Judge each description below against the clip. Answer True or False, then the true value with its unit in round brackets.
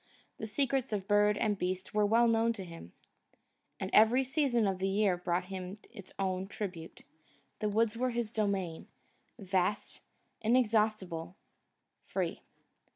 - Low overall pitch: False (205 Hz)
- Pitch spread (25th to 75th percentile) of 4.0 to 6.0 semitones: False (3.4 semitones)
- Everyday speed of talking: False (130 wpm)